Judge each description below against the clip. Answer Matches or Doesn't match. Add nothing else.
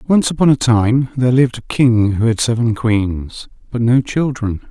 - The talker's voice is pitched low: Matches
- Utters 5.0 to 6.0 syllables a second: Doesn't match